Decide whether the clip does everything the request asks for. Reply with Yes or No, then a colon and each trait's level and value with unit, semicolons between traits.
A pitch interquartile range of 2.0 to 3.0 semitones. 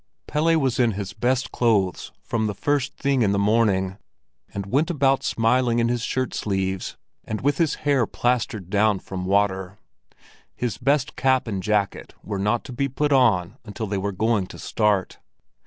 No: average, 4.6 semitones